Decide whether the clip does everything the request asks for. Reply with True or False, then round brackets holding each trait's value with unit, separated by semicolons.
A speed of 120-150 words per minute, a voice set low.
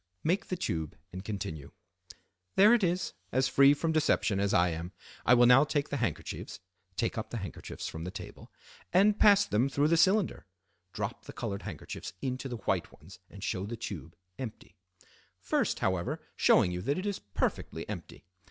False (180 wpm; 120 Hz)